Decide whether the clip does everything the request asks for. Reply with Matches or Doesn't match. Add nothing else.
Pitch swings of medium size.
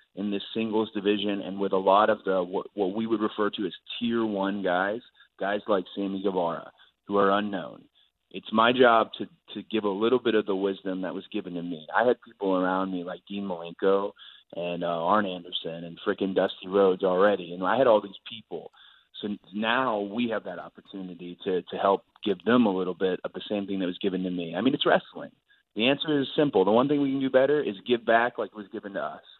Matches